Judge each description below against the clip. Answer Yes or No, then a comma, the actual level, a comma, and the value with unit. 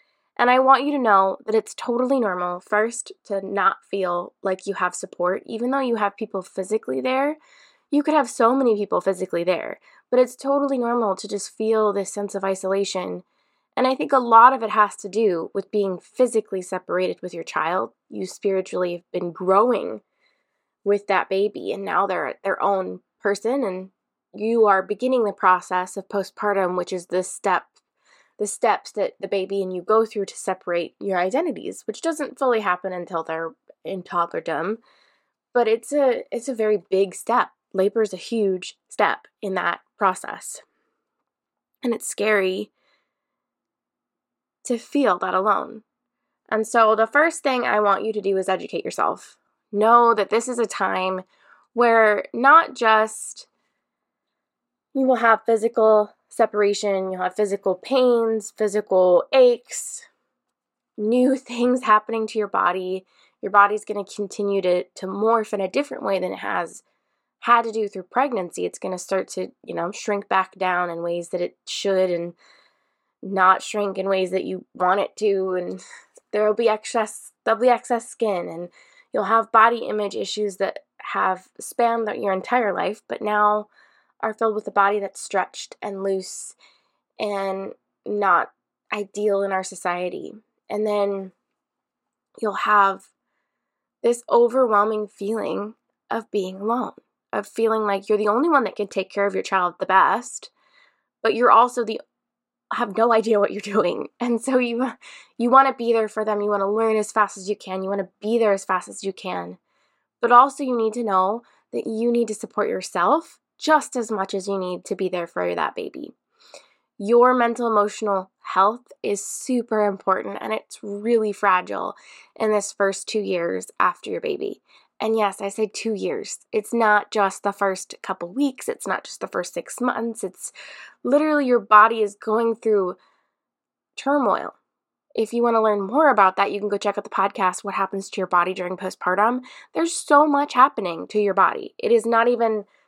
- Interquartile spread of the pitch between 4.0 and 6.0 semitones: No, average, 3.4 semitones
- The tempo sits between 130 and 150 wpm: No, average, 175 wpm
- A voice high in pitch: Yes, high, 210 Hz